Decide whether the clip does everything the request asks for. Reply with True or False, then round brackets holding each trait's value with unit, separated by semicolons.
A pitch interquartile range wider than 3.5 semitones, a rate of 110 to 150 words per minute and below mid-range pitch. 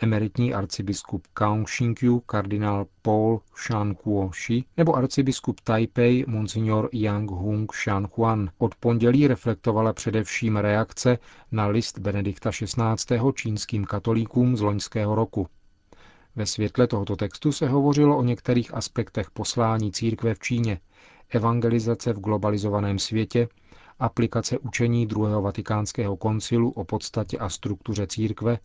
False (2.4 semitones; 115 wpm; 110 Hz)